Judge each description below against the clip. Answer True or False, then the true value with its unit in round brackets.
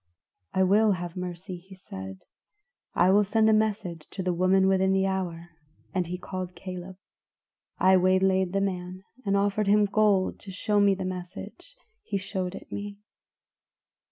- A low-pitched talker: False (190 Hz)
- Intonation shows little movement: True (1.5 semitones)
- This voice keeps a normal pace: True (160 wpm)